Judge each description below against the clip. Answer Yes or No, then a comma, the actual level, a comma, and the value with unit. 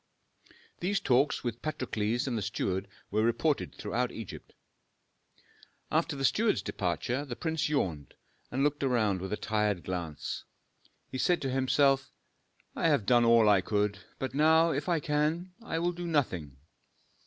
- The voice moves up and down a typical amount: No, wide, 6.4 semitones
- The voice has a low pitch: Yes, low, 130 Hz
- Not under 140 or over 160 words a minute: Yes, average, 155 wpm